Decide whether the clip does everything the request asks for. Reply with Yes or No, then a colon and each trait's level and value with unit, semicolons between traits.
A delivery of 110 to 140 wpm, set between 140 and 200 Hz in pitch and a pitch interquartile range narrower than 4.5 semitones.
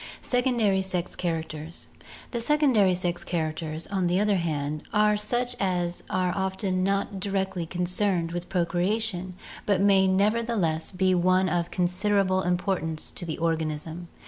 Yes: slow, 135 wpm; medium, 185 Hz; narrow, 2.6 semitones